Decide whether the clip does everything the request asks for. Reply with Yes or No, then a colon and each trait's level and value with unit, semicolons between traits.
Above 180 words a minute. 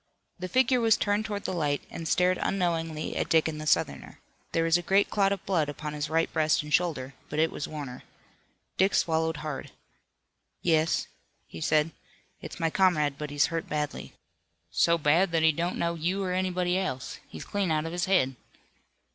Yes: average, 190 wpm